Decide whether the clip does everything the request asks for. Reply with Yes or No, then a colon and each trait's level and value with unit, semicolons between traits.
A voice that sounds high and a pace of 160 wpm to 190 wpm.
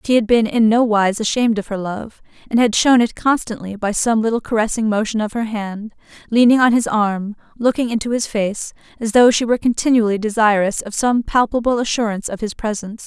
No: high, 220 Hz; average, 200 wpm